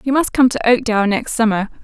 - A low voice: No, high, 235 Hz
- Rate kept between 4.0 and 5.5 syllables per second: No, 6.3 syllables/s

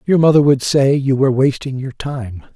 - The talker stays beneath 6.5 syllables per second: Yes, 5.1 syllables/s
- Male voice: Yes, male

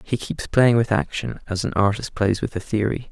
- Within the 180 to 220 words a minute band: No, fast, 230 wpm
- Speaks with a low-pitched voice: Yes, low, 110 Hz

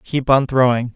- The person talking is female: No, male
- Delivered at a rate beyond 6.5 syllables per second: No, 4.7 syllables/s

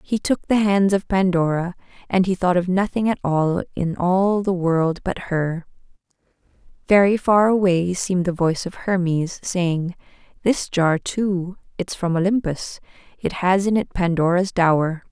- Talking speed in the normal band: Yes, average, 160 wpm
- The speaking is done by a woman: Yes, female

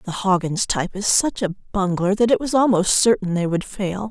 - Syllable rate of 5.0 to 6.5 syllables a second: Yes, 5.3 syllables/s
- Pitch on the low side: No, high, 200 Hz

